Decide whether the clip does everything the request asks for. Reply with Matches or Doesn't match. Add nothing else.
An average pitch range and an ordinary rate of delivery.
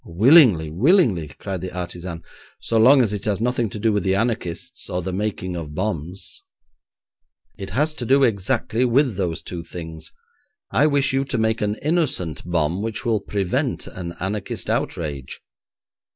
Doesn't match